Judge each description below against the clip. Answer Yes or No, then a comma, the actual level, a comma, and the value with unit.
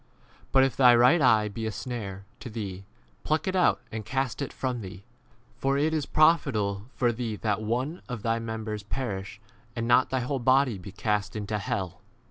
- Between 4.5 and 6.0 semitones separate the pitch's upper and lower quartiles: No, average, 4.1 semitones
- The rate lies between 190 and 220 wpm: Yes, average, 200 wpm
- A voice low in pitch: Yes, low, 115 Hz